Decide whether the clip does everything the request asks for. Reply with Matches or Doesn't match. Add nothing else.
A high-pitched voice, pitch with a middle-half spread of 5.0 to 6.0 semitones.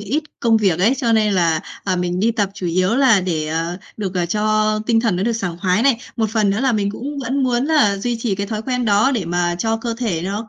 Doesn't match